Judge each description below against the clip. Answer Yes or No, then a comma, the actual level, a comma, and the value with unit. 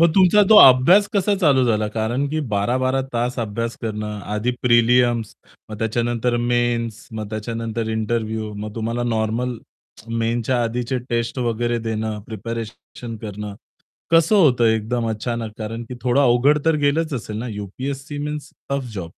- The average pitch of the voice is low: Yes, low, 120 Hz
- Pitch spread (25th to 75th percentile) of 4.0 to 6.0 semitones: No, average, 2.8 semitones